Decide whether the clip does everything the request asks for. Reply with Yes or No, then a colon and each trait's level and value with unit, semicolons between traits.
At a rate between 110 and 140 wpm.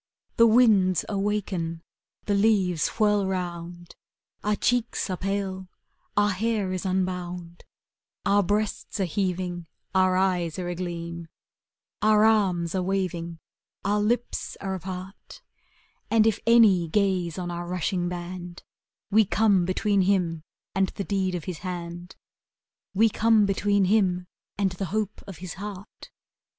Yes: slow, 135 wpm